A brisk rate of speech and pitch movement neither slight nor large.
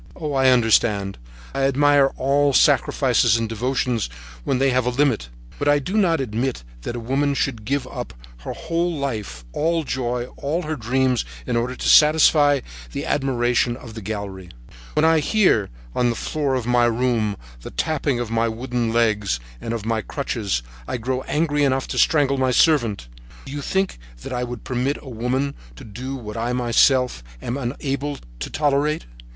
No: average, 180 wpm; average, 3.6 semitones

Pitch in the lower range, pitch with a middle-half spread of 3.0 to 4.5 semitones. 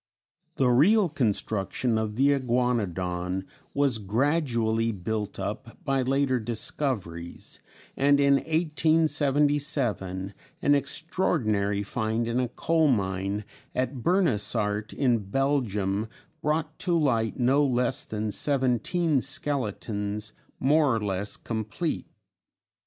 No: low, 125 Hz; average, 5.3 semitones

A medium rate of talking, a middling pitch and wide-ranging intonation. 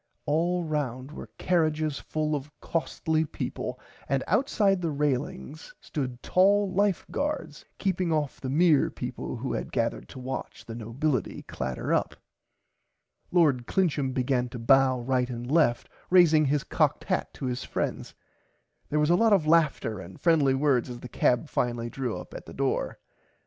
No: average, 165 wpm; medium, 145 Hz; average, 4.7 semitones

